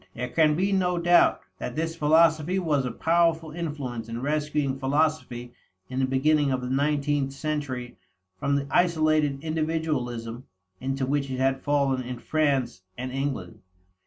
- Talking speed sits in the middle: Yes, average, 150 wpm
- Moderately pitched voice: Yes, medium, 145 Hz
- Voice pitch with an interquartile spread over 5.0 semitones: No, average, 3.1 semitones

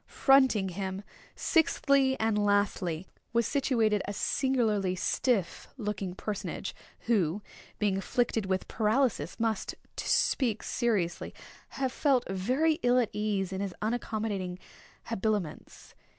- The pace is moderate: No, slow, 115 wpm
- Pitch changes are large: No, average, 4.1 semitones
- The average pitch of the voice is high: Yes, high, 215 Hz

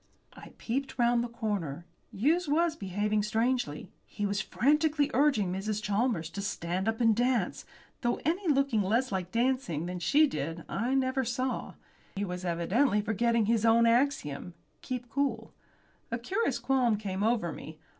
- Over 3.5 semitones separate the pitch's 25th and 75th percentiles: Yes, average, 5.1 semitones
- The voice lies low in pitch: No, high, 230 Hz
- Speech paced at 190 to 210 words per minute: No, average, 155 wpm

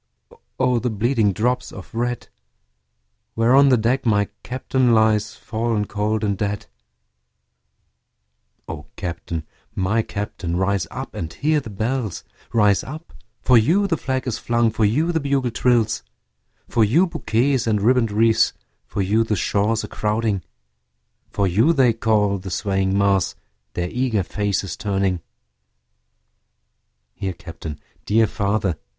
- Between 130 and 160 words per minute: Yes, average, 140 wpm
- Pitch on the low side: Yes, low, 110 Hz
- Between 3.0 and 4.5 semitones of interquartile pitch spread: Yes, average, 3.6 semitones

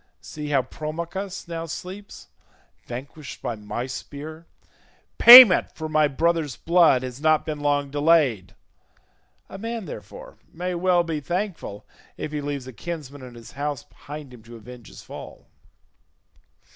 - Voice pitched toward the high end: No, medium, 150 Hz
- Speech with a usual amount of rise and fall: Yes, average, 4.2 semitones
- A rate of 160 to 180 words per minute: No, average, 145 wpm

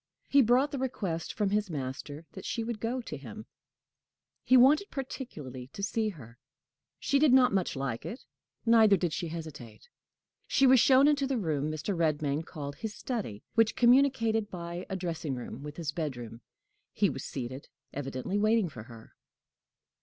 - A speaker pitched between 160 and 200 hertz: Yes, medium, 185 Hz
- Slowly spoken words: No, average, 170 wpm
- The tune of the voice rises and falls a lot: Yes, wide, 8.5 semitones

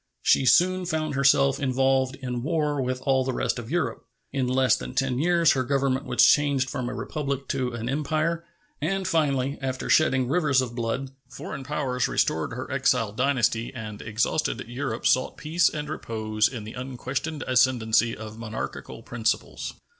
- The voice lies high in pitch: No, low, 130 Hz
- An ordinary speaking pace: Yes, average, 165 wpm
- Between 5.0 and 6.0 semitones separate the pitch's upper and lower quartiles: No, average, 3.1 semitones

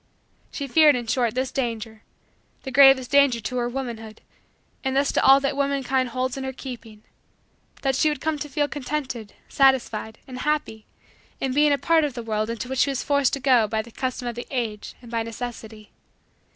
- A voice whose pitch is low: No, very high, 255 Hz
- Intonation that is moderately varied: Yes, average, 3.1 semitones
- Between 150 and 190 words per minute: No, average, 200 wpm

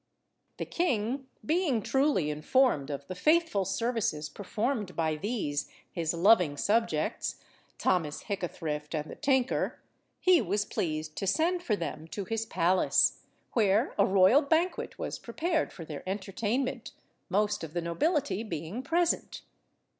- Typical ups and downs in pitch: No, wide, 8.0 semitones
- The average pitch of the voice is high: Yes, high, 205 Hz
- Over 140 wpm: No, slow, 135 wpm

